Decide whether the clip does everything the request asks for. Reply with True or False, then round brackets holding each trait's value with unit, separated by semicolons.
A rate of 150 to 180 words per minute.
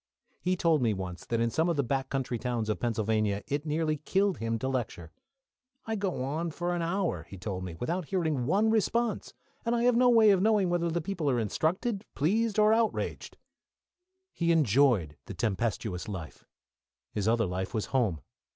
False (190 wpm)